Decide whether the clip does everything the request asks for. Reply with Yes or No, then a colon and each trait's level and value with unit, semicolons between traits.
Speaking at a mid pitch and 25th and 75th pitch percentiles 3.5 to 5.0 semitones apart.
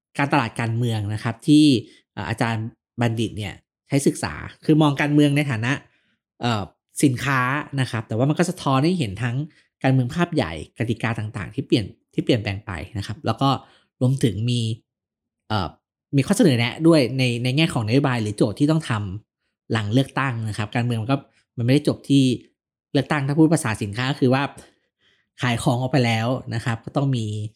No: low, 125 Hz; average, 4.1 semitones